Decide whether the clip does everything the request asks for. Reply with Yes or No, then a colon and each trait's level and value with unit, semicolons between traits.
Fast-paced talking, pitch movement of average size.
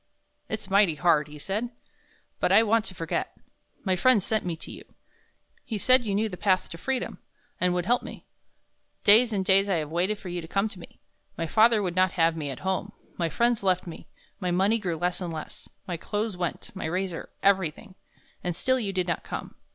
Yes: fast, 215 wpm; average, 3.5 semitones